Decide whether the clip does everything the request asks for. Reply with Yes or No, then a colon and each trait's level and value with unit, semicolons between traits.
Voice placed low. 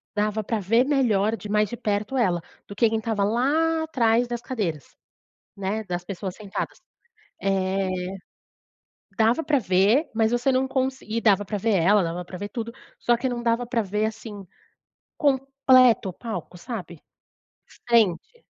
No: high, 220 Hz